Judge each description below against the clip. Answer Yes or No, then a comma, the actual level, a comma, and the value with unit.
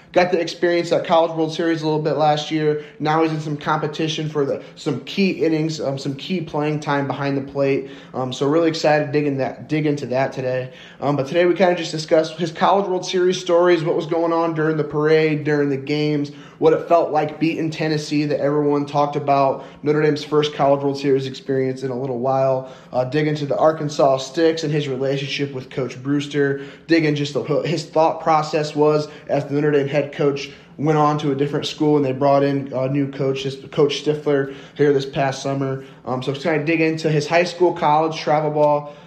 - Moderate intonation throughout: No, narrow, 2.2 semitones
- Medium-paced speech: No, fast, 220 wpm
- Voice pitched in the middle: Yes, medium, 150 Hz